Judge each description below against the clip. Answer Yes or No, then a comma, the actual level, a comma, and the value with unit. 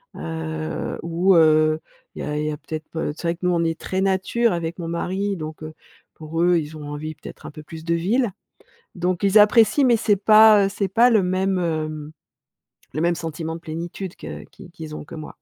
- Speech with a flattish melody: No, average, 3.6 semitones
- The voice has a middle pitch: Yes, medium, 170 Hz